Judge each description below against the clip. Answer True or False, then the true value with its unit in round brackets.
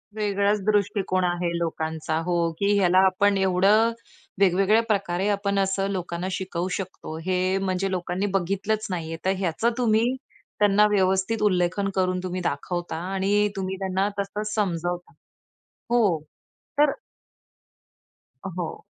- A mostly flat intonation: True (2.1 semitones)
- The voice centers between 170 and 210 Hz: True (190 Hz)